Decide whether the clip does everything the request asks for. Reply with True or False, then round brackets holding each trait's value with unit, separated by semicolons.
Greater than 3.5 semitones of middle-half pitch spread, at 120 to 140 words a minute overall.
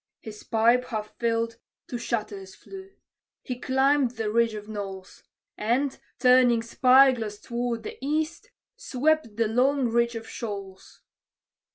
False (3.1 semitones; 135 wpm)